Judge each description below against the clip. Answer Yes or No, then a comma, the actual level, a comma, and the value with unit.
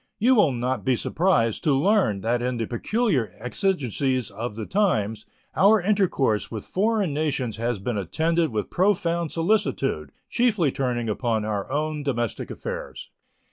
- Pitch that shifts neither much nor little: No, wide, 8.2 semitones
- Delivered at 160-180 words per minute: No, average, 145 wpm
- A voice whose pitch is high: No, low, 135 Hz